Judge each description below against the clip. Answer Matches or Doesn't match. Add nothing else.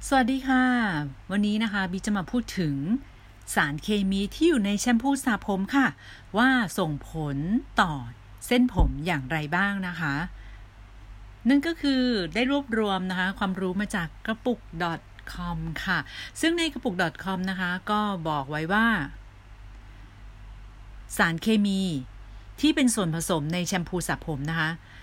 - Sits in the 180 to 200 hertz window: Matches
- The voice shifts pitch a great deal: Matches